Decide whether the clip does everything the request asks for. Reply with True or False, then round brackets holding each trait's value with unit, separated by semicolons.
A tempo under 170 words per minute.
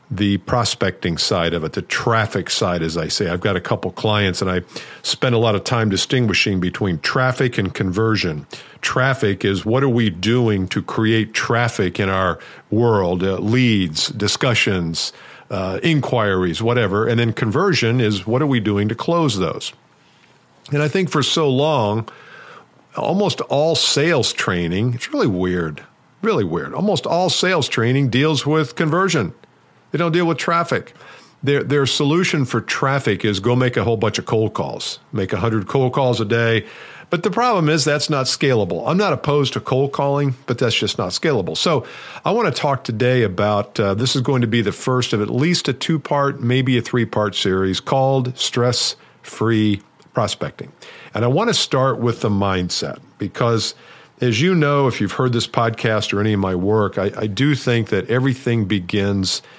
False (180 wpm)